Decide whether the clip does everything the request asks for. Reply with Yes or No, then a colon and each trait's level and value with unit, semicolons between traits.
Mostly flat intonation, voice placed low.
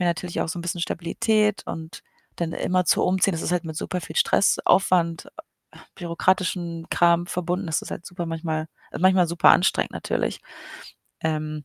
No: narrow, 1.8 semitones; medium, 175 Hz